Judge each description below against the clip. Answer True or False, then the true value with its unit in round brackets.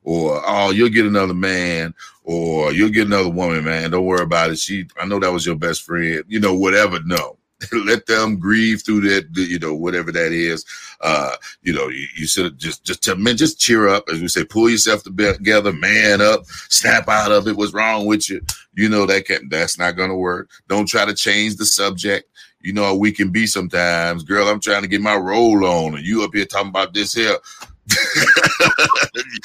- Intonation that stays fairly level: False (3.3 semitones)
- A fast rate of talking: True (210 wpm)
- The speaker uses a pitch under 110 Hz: True (100 Hz)